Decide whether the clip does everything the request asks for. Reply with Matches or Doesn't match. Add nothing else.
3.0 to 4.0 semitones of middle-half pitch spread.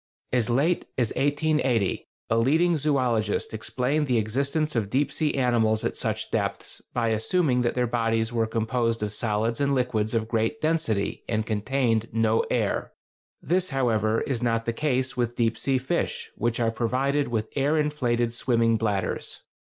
Matches